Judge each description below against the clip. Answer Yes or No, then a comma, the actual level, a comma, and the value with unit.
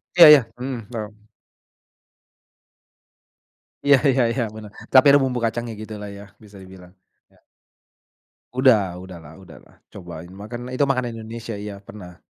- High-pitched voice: No, low, 110 Hz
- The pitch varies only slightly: No, average, 3.9 semitones